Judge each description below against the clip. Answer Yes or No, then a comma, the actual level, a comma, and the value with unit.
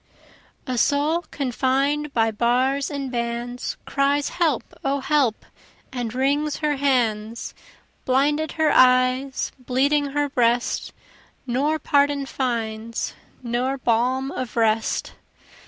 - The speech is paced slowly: Yes, slow, 105 wpm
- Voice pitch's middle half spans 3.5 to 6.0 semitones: No, average, 3.0 semitones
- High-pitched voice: Yes, very high, 265 Hz